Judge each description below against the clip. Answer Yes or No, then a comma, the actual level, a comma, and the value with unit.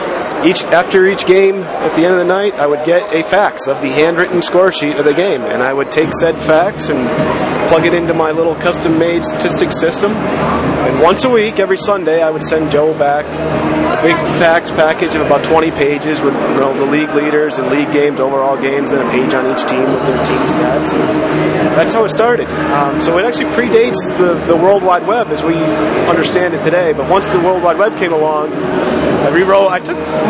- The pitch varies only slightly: No, average, 3.4 semitones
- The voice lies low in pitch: No, medium, 160 Hz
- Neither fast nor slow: No, fast, 220 wpm